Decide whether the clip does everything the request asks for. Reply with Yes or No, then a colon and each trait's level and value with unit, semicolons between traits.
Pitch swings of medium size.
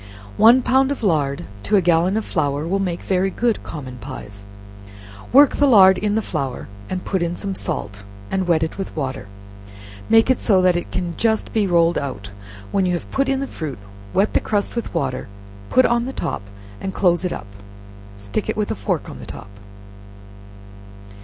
No: wide, 6.4 semitones